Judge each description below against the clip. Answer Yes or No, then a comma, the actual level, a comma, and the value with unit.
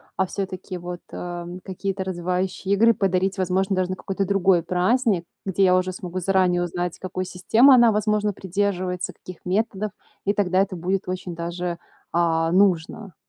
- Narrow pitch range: Yes, narrow, 1.8 semitones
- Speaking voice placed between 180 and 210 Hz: Yes, medium, 185 Hz